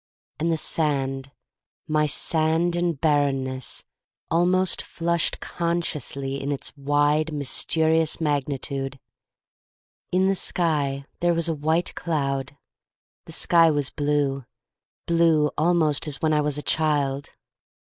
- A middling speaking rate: No, slow, 130 wpm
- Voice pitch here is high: No, medium, 150 Hz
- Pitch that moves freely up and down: No, average, 3.0 semitones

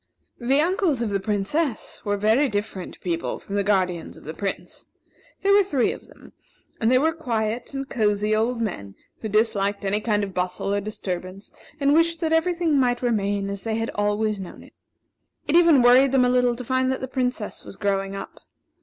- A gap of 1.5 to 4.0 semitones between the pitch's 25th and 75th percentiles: No, average, 4.7 semitones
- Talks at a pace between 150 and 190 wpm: No, fast, 205 wpm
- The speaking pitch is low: No, high, 220 Hz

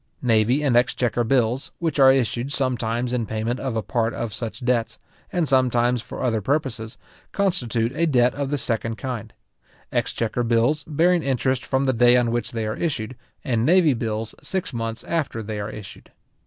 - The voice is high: No, low, 120 Hz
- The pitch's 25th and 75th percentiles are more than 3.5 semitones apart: No, average, 3.0 semitones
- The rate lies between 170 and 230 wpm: Yes, average, 180 wpm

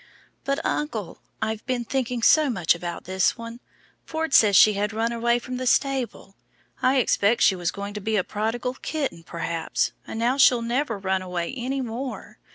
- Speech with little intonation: No, average, 4.3 semitones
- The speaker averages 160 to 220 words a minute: Yes, average, 180 wpm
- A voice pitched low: No, high, 230 Hz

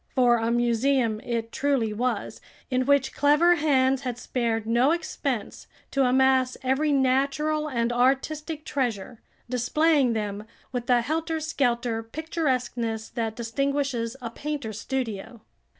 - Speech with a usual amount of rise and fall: Yes, average, 3.4 semitones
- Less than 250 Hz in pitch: No, very high, 255 Hz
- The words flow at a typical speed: No, slow, 125 wpm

